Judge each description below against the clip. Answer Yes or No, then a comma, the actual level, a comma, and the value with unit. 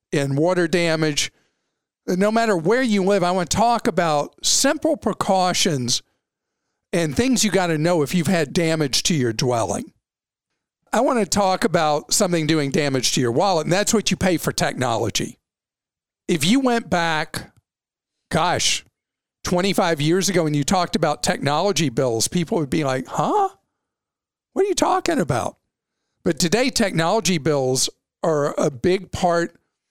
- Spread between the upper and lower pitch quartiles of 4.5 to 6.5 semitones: Yes, average, 5.2 semitones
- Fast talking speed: No, average, 155 wpm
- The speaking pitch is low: No, medium, 180 Hz